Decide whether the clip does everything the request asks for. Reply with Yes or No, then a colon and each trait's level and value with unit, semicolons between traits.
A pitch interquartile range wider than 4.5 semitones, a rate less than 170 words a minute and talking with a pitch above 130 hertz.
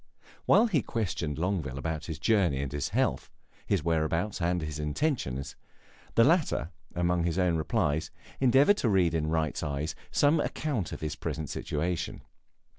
No: average, 5.3 semitones; average, 155 wpm; very low, 85 Hz